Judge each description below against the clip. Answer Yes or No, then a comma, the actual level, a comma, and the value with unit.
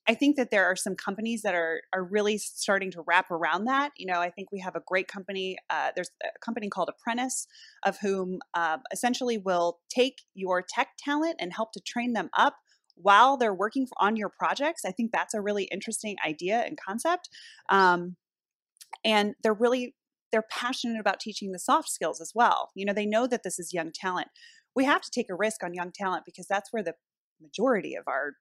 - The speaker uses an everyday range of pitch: Yes, average, 4.9 semitones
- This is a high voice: Yes, high, 210 Hz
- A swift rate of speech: Yes, fast, 210 wpm